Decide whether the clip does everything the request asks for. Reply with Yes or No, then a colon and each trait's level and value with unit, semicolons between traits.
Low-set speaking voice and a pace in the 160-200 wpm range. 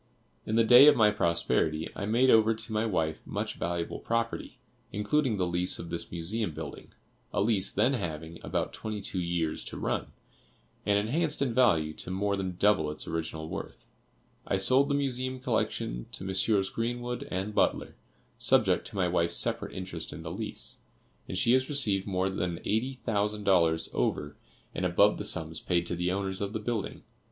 Yes: low, 100 Hz; average, 180 wpm